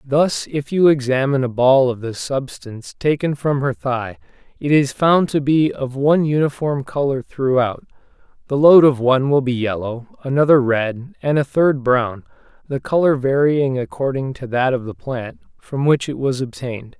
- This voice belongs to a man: Yes, male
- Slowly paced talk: No, average, 175 wpm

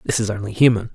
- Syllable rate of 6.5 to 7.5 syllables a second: Yes, 7.1 syllables/s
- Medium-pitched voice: No, low, 110 Hz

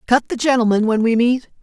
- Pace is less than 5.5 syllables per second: No, 5.7 syllables/s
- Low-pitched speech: No, high, 235 Hz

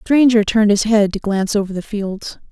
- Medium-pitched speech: No, high, 210 Hz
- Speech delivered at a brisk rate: Yes, fast, 240 wpm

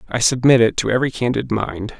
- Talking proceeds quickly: Yes, fast, 210 wpm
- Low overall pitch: Yes, low, 120 Hz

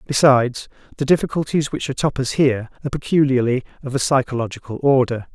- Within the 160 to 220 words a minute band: No, average, 145 wpm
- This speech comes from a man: Yes, male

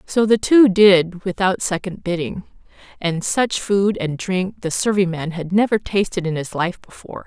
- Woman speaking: Yes, female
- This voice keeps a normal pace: Yes, average, 180 wpm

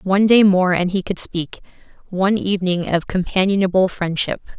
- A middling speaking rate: Yes, average, 145 wpm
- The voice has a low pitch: No, medium, 185 Hz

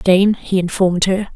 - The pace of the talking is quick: No, average, 180 wpm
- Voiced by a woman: Yes, female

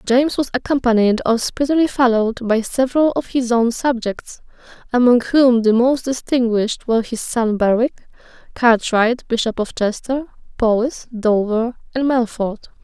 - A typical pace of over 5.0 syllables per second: No, 4.9 syllables/s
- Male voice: No, female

